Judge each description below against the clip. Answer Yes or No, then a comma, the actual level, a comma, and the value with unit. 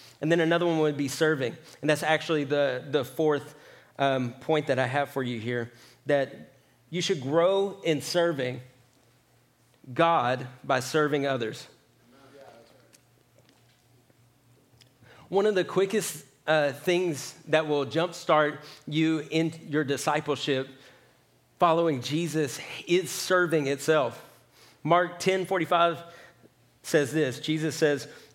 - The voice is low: No, medium, 150 Hz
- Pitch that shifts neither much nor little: Yes, average, 3.8 semitones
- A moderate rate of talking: No, slow, 120 wpm